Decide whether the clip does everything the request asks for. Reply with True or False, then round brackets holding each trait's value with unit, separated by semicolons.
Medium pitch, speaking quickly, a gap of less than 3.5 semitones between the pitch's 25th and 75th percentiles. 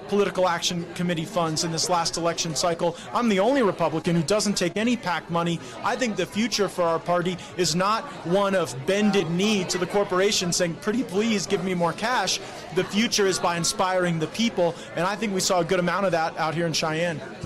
True (180 Hz; 215 wpm; 2.8 semitones)